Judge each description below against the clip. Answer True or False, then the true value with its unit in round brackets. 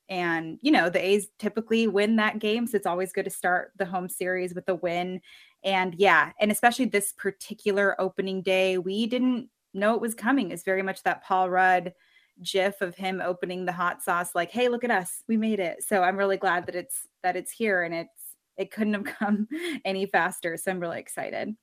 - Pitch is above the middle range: True (195 Hz)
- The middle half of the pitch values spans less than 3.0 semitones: True (2.6 semitones)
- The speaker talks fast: True (215 wpm)